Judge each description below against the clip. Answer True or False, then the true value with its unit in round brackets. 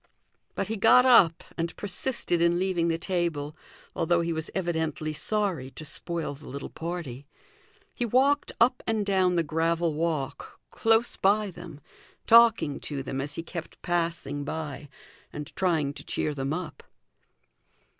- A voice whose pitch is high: False (170 Hz)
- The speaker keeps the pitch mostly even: False (3.9 semitones)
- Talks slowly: False (150 wpm)